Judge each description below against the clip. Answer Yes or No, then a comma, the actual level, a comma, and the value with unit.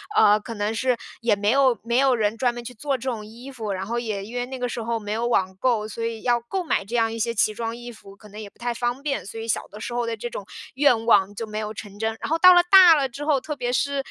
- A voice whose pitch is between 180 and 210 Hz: No, high, 235 Hz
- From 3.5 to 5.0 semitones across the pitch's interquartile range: No, average, 3.0 semitones